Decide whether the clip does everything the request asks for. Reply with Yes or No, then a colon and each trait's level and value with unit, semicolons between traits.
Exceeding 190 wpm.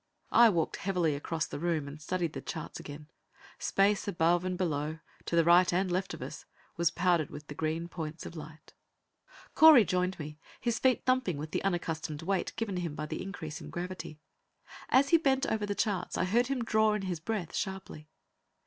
Yes: average, 200 wpm